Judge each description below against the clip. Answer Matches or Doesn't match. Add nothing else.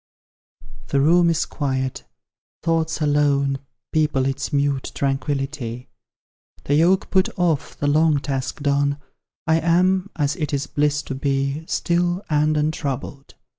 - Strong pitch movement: Doesn't match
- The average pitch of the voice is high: Doesn't match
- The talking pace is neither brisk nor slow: Doesn't match